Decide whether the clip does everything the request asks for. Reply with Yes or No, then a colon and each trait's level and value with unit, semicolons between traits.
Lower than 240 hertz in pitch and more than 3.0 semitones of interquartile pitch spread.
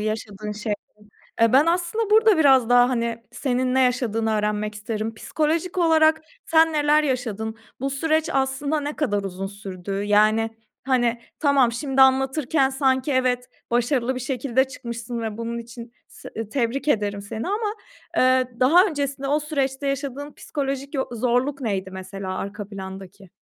No: very high, 255 Hz; average, 4.3 semitones